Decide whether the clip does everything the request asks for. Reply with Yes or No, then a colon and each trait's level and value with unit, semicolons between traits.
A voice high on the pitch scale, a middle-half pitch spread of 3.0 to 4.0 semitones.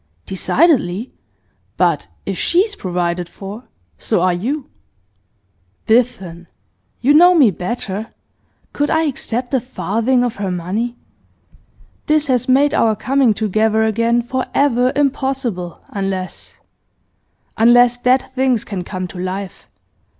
No: high, 235 Hz; average, 5.3 semitones